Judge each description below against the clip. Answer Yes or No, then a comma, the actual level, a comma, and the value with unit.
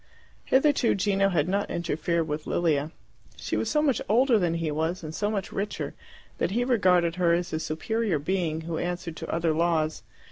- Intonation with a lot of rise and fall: No, average, 4.0 semitones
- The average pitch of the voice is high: No, medium, 175 Hz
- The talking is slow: No, average, 185 wpm